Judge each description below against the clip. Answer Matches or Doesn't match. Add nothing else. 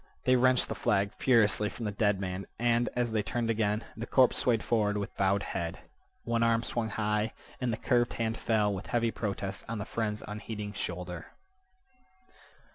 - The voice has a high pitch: Doesn't match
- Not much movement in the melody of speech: Matches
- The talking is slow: Doesn't match